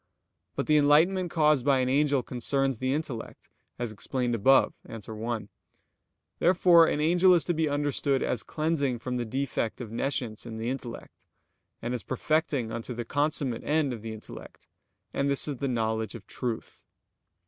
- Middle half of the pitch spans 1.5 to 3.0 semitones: No, average, 4.2 semitones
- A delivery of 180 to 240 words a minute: No, average, 170 wpm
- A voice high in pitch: No, low, 130 Hz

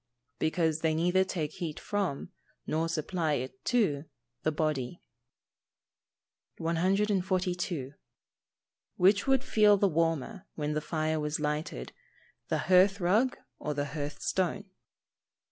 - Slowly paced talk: Yes, slow, 120 wpm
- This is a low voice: No, medium, 165 Hz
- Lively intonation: No, average, 3.9 semitones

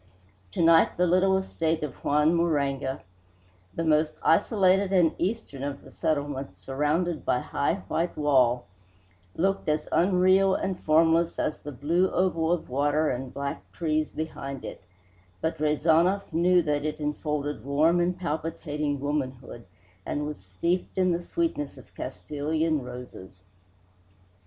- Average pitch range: Yes, average, 3.3 semitones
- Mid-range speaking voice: Yes, medium, 155 Hz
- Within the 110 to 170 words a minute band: Yes, average, 140 wpm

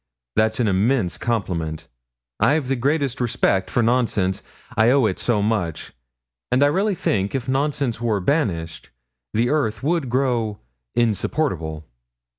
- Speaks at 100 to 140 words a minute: Yes, slow, 135 wpm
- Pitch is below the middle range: Yes, low, 115 Hz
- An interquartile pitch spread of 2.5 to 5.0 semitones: No, wide, 5.4 semitones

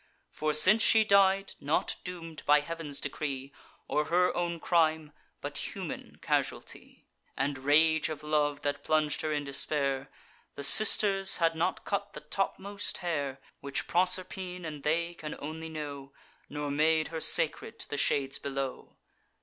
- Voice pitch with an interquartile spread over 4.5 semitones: No, average, 3.4 semitones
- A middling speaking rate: Yes, average, 150 wpm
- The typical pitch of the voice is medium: Yes, medium, 155 Hz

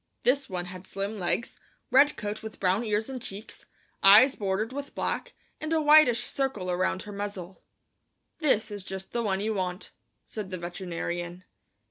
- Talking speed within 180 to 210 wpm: No, average, 165 wpm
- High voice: Yes, high, 205 Hz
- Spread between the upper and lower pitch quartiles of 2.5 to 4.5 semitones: Yes, average, 4.2 semitones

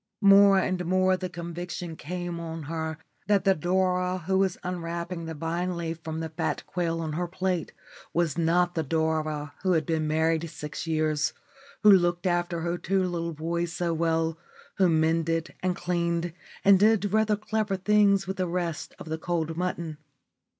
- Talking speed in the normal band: Yes, average, 170 wpm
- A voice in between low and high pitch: Yes, medium, 170 Hz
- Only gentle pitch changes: Yes, narrow, 2.1 semitones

